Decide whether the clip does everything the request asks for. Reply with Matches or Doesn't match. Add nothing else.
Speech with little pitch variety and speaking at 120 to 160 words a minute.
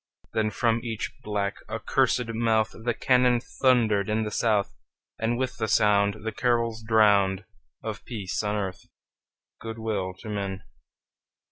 Matches